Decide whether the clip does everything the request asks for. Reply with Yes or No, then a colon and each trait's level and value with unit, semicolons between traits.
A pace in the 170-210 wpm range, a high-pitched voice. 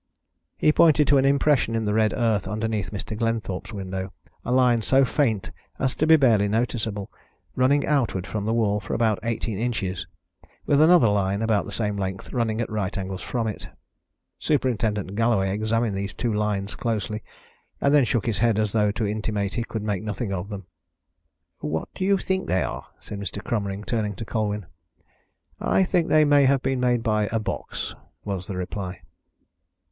No: average, 185 wpm; low, 110 Hz